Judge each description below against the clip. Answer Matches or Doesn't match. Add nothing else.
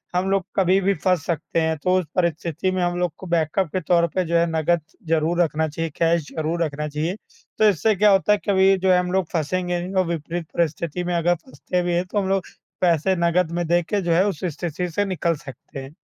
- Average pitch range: Doesn't match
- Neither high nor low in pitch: Matches